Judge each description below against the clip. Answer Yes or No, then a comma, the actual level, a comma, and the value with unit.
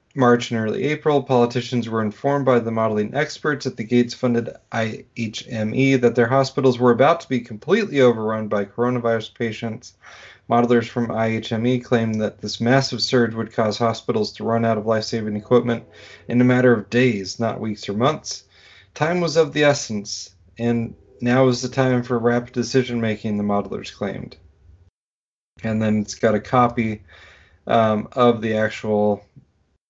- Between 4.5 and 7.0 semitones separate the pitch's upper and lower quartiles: No, narrow, 2.6 semitones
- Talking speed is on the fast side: No, average, 165 wpm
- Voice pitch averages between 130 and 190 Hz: No, low, 115 Hz